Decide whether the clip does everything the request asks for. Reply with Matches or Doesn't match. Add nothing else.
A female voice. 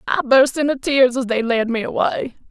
Matches